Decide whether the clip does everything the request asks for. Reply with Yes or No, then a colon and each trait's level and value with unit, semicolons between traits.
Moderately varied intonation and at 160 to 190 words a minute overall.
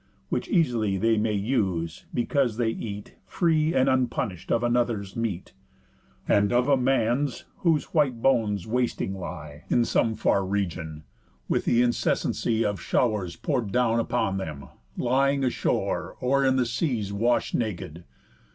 No: average, 4.1 semitones; average, 140 wpm